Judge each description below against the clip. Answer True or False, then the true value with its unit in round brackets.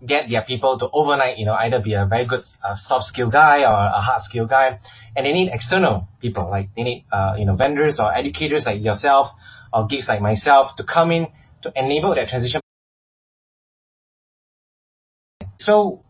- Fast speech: False (185 wpm)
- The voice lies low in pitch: True (125 Hz)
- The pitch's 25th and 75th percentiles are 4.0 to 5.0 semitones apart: True (4.7 semitones)